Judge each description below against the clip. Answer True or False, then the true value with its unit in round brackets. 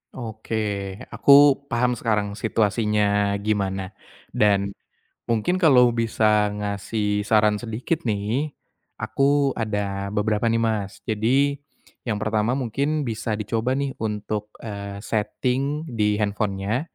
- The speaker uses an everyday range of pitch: True (3.0 semitones)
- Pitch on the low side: True (110 Hz)